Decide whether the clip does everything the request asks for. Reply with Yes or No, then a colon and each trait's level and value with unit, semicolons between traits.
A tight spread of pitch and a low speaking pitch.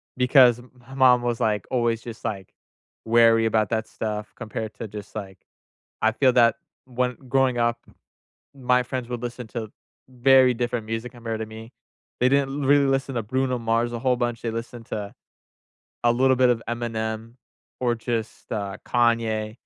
Yes: narrow, 2.1 semitones; low, 120 Hz